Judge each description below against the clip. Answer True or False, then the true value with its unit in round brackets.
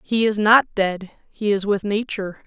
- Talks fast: False (195 wpm)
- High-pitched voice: True (205 Hz)